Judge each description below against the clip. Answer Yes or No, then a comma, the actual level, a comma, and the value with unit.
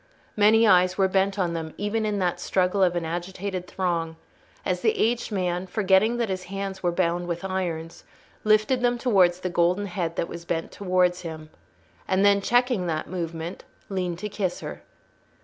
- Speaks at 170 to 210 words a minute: Yes, average, 180 wpm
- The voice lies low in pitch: No, medium, 185 Hz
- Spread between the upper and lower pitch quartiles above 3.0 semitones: No, average, 2.7 semitones